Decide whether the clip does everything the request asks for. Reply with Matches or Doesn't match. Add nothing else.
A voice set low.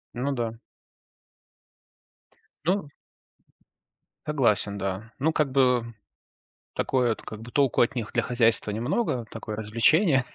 Matches